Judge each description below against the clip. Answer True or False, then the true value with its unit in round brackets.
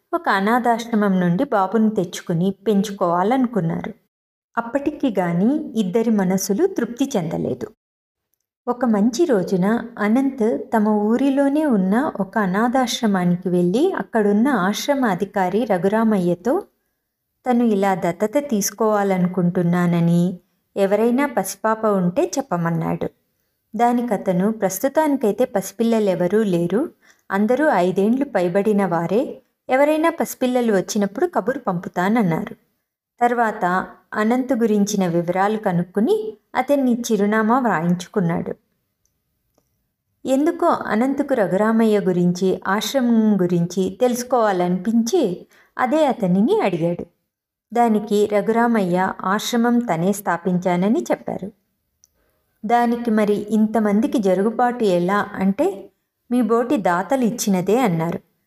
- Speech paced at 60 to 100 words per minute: True (85 wpm)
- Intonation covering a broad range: False (4.0 semitones)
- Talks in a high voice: True (215 Hz)